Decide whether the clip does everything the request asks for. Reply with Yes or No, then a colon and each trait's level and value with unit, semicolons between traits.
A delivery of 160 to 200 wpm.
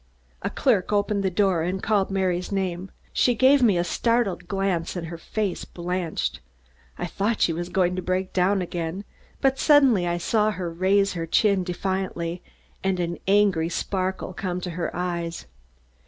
Yes: average, 170 wpm